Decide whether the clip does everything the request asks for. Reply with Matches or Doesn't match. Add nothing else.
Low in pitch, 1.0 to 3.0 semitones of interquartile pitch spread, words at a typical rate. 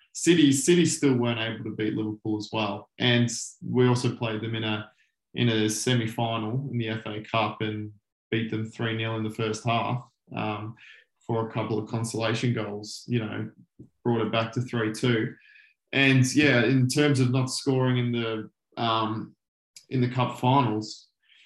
Matches